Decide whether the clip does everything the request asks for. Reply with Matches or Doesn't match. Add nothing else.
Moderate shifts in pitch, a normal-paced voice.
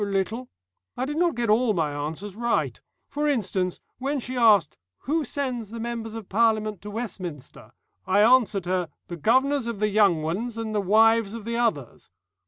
Matches